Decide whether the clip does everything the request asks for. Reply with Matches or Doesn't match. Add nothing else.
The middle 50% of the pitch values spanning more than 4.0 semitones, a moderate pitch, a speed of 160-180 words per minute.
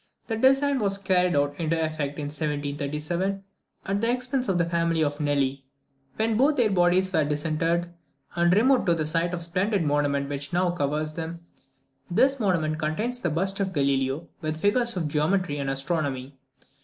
Matches